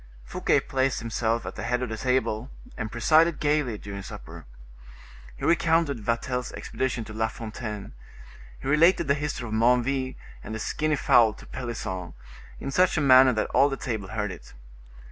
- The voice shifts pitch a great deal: No, average, 3.9 semitones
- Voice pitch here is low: Yes, low, 125 Hz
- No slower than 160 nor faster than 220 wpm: Yes, average, 170 wpm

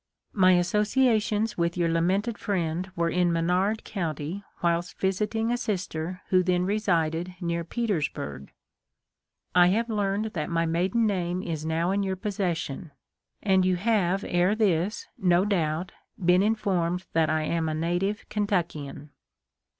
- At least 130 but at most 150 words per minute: Yes, average, 145 wpm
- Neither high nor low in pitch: Yes, medium, 180 Hz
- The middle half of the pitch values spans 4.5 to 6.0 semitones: No, average, 3.3 semitones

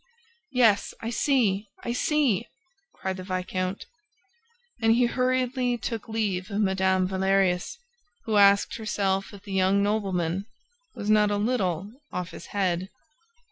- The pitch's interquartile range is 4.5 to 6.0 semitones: No, average, 3.1 semitones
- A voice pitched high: Yes, high, 200 Hz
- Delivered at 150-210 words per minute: No, slow, 135 wpm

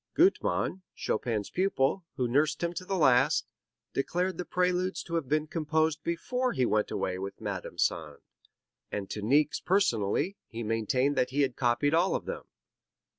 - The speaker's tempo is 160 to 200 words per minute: Yes, average, 165 wpm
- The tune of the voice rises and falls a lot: Yes, wide, 7.1 semitones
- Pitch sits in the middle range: Yes, medium, 145 Hz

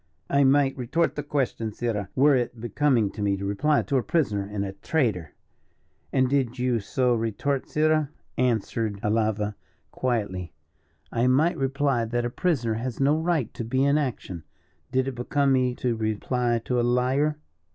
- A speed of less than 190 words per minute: Yes, average, 165 wpm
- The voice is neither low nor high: No, low, 125 Hz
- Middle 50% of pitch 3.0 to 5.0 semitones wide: Yes, average, 3.9 semitones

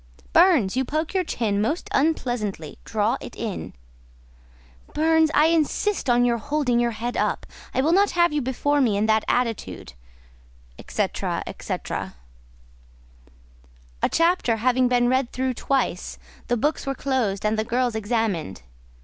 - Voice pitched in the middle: No, high, 245 Hz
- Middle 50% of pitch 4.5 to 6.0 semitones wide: Yes, average, 5.2 semitones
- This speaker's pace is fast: No, average, 145 wpm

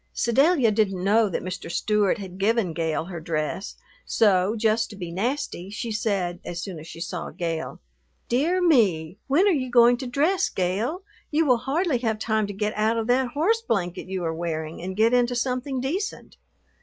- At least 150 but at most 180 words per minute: No, average, 190 wpm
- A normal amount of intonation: No, wide, 5.7 semitones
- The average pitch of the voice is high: Yes, high, 215 Hz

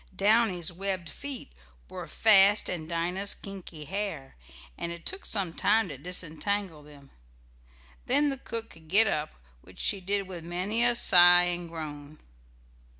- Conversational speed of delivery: Yes, average, 150 wpm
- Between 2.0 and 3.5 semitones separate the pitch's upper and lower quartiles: No, average, 3.9 semitones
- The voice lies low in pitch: No, medium, 180 Hz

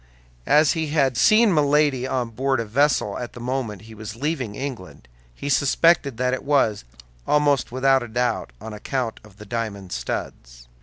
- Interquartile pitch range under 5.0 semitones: Yes, average, 4.3 semitones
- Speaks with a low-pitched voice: Yes, low, 125 Hz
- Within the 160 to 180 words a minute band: Yes, average, 170 wpm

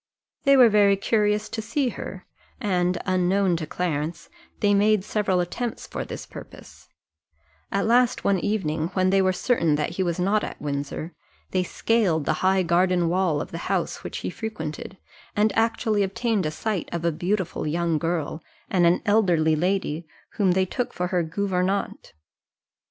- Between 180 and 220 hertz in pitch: Yes, medium, 185 Hz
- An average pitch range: Yes, average, 3.6 semitones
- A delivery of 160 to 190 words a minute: Yes, average, 170 wpm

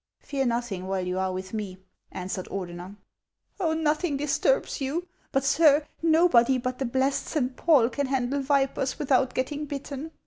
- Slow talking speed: No, average, 170 wpm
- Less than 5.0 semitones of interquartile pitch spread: Yes, average, 4.3 semitones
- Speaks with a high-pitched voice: Yes, very high, 265 Hz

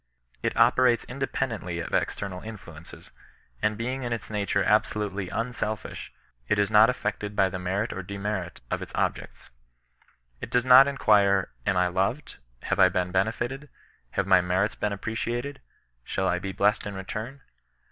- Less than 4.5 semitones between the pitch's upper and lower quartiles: Yes, average, 3.7 semitones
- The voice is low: Yes, low, 105 Hz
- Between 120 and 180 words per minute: Yes, average, 170 wpm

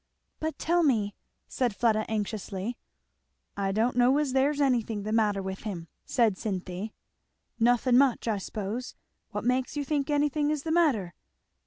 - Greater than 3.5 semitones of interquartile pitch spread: Yes, average, 5.1 semitones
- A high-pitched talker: Yes, high, 235 Hz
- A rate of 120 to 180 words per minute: Yes, average, 155 wpm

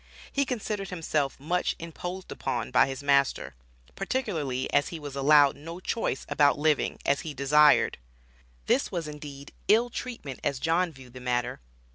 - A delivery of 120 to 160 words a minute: Yes, average, 155 wpm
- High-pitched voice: No, medium, 150 Hz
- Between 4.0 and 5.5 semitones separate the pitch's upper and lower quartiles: Yes, average, 4.4 semitones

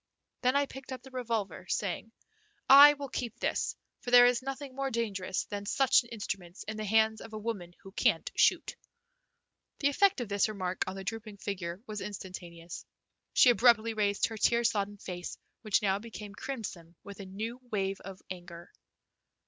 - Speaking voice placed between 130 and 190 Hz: No, high, 215 Hz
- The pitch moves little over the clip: No, average, 4.0 semitones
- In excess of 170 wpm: Yes, average, 180 wpm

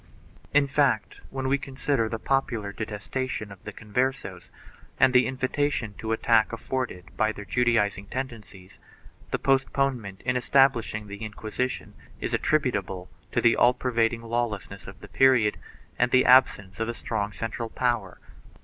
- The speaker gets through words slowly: No, average, 150 wpm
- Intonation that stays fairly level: No, average, 3.7 semitones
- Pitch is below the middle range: Yes, low, 115 Hz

